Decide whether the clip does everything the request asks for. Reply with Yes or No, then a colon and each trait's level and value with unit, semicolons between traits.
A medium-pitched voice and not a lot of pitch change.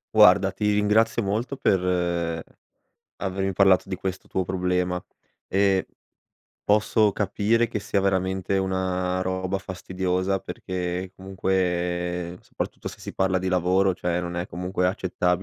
No: very low, 95 Hz; narrow, 1.3 semitones